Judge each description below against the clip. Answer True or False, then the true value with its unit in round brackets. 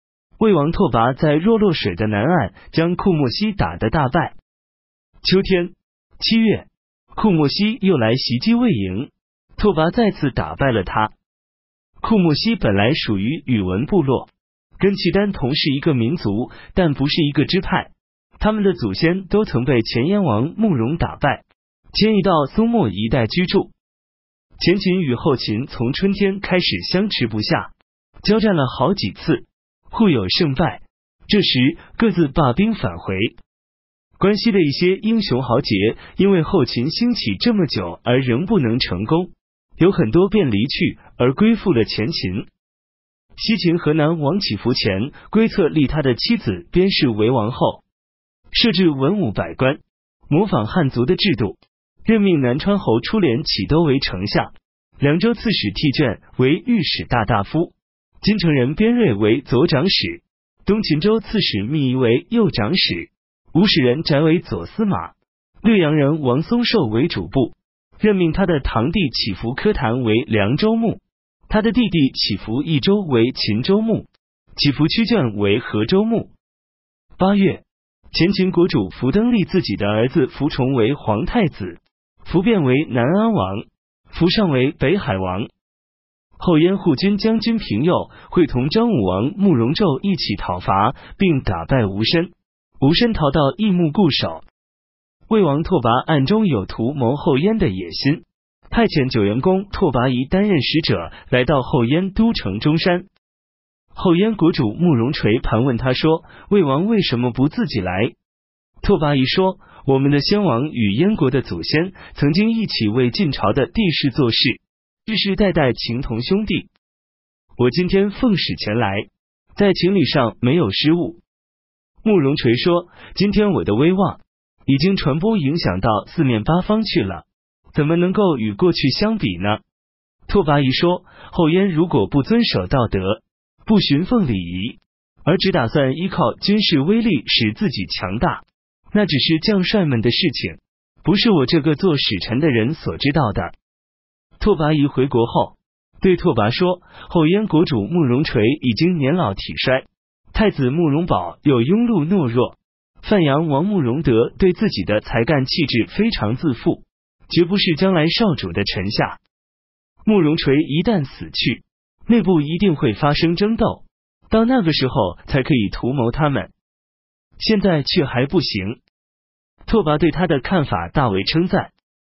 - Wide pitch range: True (8.7 semitones)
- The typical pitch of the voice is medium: True (155 Hz)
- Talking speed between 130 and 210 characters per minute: False (225 characters per minute)